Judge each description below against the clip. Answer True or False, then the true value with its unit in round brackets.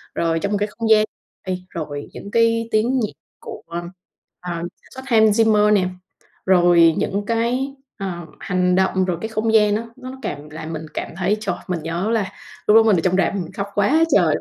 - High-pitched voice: True (200 Hz)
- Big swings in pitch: False (4.1 semitones)